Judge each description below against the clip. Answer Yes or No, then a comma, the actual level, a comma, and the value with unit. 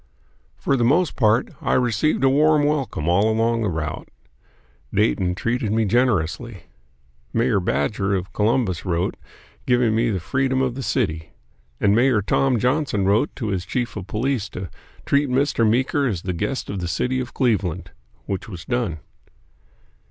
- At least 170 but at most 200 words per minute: No, average, 160 wpm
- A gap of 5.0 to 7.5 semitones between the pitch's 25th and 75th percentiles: Yes, wide, 5.4 semitones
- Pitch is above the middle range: No, low, 115 Hz